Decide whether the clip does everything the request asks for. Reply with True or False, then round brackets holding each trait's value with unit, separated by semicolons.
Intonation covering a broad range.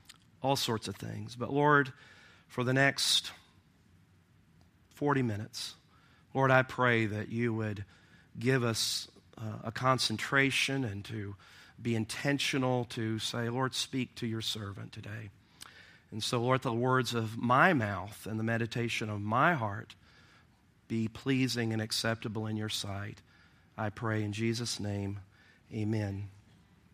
False (3.4 semitones)